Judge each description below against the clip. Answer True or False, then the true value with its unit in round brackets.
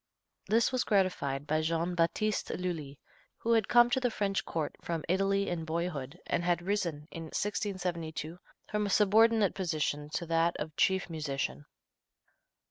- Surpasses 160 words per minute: False (150 wpm)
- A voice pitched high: False (175 Hz)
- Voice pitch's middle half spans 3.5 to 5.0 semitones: True (4.1 semitones)